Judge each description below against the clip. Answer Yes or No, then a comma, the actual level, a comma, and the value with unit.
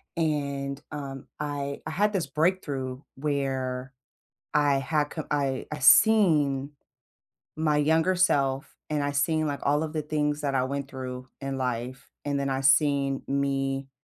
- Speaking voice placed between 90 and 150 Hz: Yes, medium, 140 Hz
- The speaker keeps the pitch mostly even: Yes, narrow, 1.8 semitones